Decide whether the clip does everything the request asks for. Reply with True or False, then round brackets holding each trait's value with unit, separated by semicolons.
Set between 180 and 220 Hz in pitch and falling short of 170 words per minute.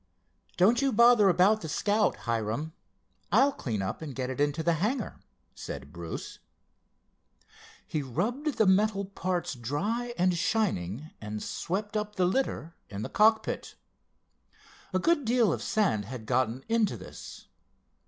True (185 Hz; 145 wpm)